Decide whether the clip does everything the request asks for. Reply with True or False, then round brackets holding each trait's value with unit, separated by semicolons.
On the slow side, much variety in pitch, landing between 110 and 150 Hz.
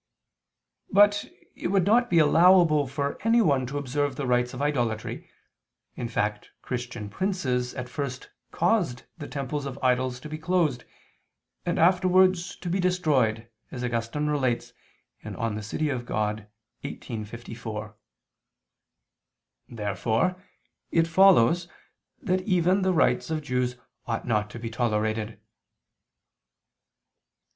True (120 wpm; 6.8 semitones; 135 Hz)